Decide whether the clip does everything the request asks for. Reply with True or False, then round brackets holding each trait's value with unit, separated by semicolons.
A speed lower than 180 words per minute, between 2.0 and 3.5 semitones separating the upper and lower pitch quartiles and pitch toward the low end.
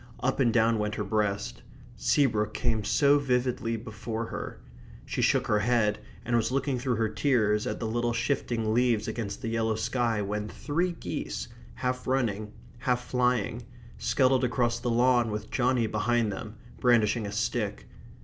True (160 wpm; 2.7 semitones; 115 Hz)